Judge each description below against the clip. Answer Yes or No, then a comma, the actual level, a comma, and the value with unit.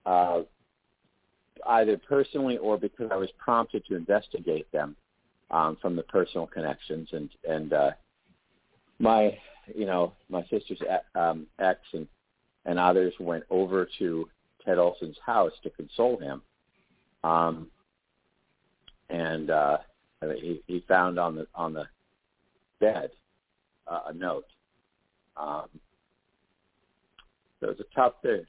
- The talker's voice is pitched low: Yes, very low, 85 Hz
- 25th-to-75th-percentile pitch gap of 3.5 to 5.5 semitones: No, average, 2.7 semitones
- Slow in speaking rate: Yes, slow, 125 wpm